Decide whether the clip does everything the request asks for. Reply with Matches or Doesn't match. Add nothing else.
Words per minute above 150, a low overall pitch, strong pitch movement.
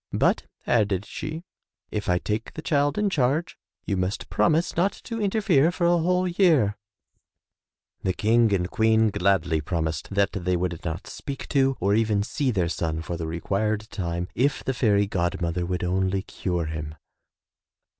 Matches